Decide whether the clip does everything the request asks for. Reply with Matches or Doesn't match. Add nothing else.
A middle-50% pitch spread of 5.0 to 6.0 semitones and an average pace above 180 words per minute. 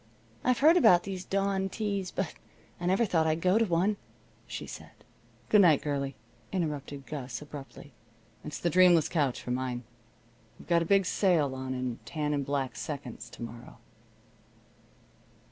Doesn't match